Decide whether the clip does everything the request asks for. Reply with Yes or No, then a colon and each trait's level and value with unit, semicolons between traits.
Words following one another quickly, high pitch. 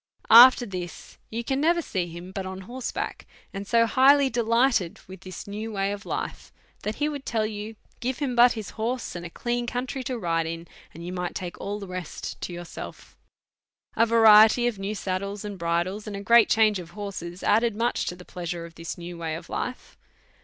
Yes: fast, 210 wpm; high, 205 Hz